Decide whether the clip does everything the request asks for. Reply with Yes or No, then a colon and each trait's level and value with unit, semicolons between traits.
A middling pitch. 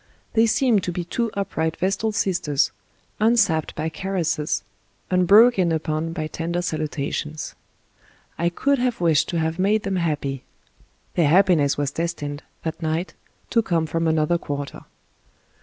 Yes: medium, 170 Hz